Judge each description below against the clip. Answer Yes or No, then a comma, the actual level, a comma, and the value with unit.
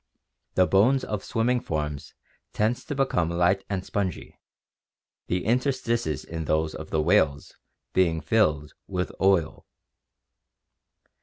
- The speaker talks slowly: Yes, slow, 120 wpm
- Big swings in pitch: Yes, wide, 6.0 semitones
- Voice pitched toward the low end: Yes, very low, 95 Hz